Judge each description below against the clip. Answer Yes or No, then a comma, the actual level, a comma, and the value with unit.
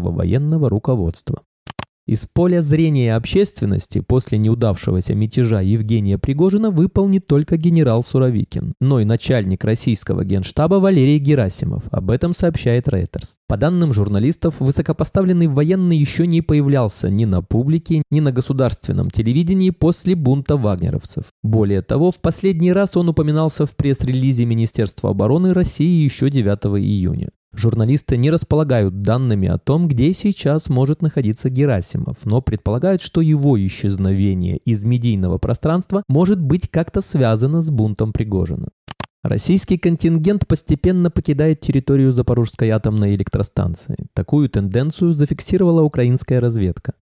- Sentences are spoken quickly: No, average, 125 wpm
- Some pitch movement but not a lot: No, wide, 6.7 semitones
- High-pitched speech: No, low, 135 Hz